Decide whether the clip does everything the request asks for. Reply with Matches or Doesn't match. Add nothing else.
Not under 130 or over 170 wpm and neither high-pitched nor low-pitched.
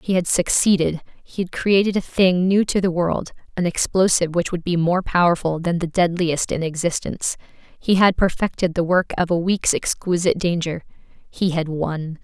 Doesn't match